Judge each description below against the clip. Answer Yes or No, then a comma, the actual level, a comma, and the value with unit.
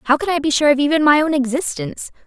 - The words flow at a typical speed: No, fast, 265 wpm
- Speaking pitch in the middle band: No, very high, 285 Hz